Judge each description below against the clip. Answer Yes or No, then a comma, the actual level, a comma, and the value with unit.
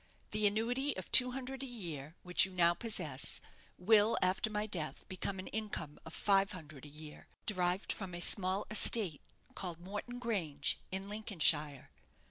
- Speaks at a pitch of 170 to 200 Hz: Yes, high, 190 Hz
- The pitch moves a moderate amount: Yes, average, 4.3 semitones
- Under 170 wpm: Yes, average, 160 wpm